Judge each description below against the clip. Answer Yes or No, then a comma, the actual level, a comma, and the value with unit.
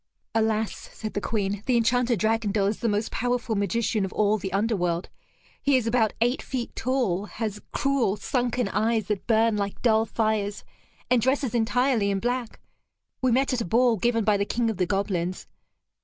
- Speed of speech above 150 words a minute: Yes, average, 180 wpm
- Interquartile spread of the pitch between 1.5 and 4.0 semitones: Yes, average, 3.0 semitones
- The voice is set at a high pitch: Yes, high, 220 Hz